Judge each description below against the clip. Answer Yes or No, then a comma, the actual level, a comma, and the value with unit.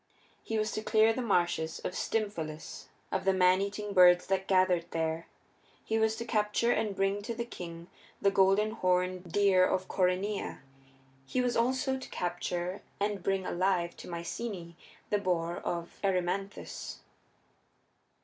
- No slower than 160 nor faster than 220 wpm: No, average, 145 wpm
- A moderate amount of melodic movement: Yes, average, 3.1 semitones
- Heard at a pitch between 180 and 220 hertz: Yes, high, 190 Hz